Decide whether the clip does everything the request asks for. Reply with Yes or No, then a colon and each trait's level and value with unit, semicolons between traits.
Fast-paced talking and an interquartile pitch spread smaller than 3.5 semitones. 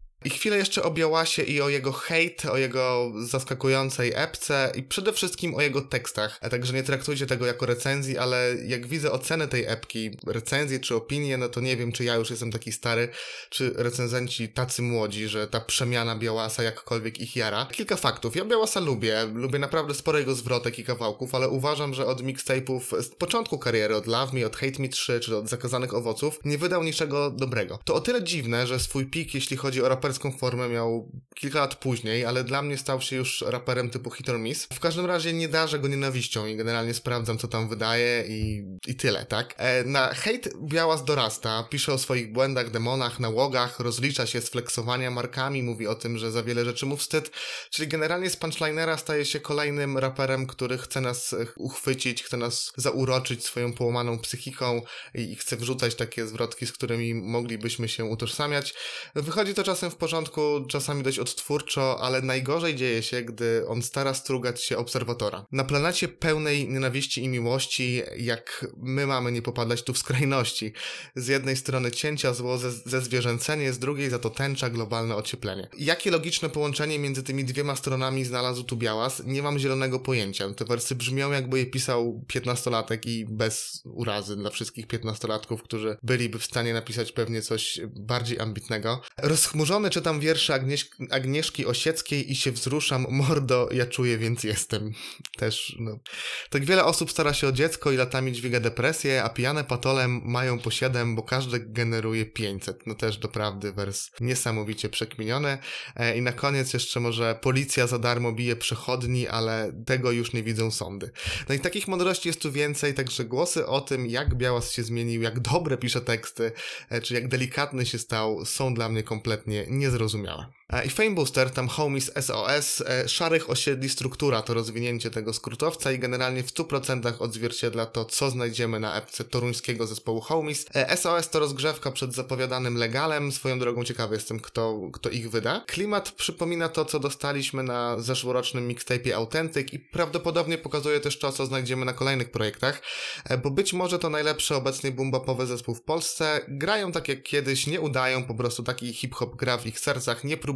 Yes: fast, 175 wpm; average, 3.1 semitones